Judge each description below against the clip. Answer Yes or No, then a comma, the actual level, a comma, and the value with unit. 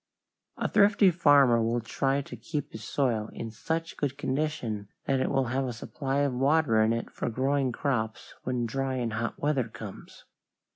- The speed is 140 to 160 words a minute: No, average, 180 wpm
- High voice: No, low, 130 Hz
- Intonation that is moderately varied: Yes, average, 3.7 semitones